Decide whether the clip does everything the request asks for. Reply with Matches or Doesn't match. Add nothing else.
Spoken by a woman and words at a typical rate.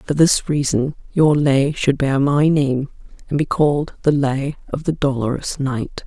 Matches